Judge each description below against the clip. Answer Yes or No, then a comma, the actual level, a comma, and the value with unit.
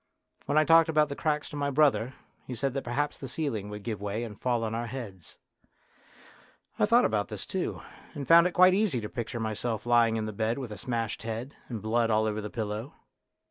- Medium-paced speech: No, fast, 220 wpm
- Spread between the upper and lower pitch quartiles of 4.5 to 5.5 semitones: Yes, average, 4.8 semitones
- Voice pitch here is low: Yes, low, 120 Hz